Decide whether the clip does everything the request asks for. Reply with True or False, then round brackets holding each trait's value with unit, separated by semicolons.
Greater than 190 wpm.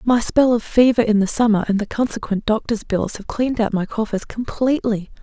True (205 wpm)